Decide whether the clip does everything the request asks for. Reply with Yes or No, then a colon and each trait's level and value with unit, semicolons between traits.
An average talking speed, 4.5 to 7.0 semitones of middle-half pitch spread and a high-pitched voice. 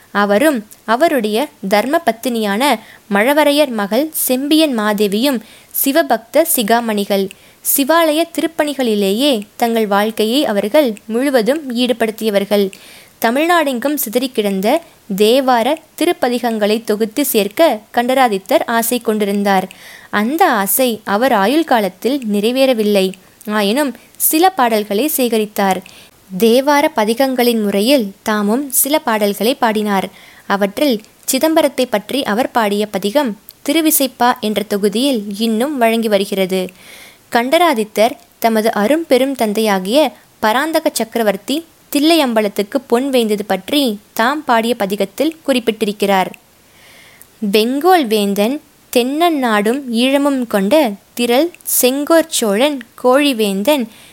Yes: average, 90 wpm; average, 5.1 semitones; high, 235 Hz